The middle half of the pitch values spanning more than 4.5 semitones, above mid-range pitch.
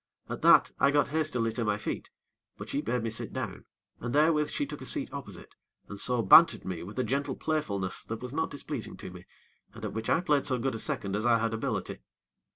No: average, 5.0 semitones; low, 120 Hz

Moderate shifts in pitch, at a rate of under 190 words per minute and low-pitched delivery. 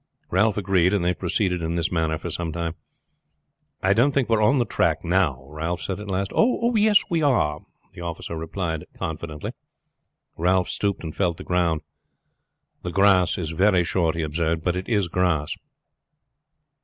Yes: average, 3.4 semitones; average, 175 wpm; very low, 90 Hz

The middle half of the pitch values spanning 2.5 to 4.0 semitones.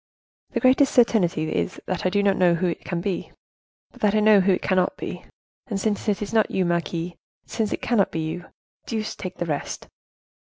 Yes: average, 3.7 semitones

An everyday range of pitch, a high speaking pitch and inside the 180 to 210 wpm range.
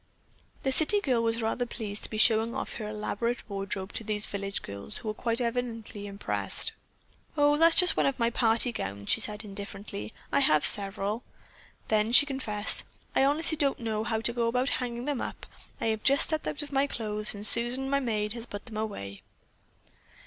Yes: average, 3.2 semitones; high, 225 Hz; average, 195 wpm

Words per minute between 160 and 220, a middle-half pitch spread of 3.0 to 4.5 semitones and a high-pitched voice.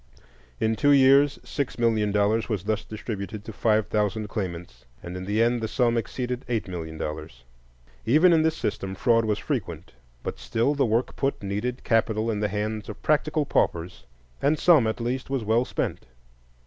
No: average, 180 wpm; average, 3.5 semitones; low, 110 Hz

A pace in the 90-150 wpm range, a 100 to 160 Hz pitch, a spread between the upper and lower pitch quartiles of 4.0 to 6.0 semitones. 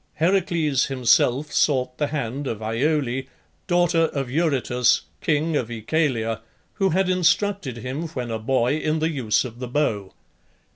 Yes: average, 145 wpm; medium, 140 Hz; average, 4.7 semitones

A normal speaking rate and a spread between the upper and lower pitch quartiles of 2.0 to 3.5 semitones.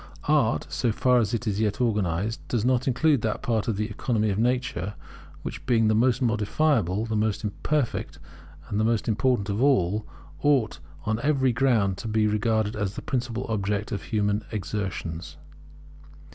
Yes: average, 170 wpm; average, 3.0 semitones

